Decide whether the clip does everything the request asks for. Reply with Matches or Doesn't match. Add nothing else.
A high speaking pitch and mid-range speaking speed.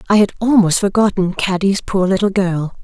Matches